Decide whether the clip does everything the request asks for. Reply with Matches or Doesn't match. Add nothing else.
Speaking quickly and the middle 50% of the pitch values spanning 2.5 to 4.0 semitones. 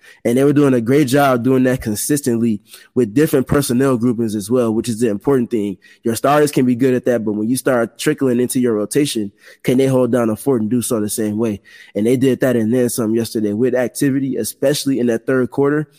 Matches